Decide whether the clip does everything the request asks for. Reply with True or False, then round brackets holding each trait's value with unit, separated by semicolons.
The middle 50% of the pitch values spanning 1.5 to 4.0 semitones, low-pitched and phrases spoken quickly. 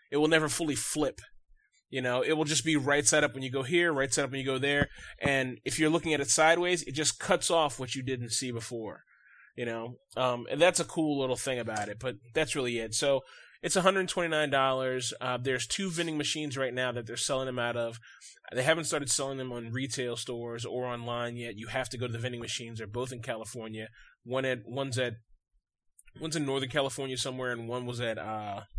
True (3.7 semitones; 130 Hz; 225 wpm)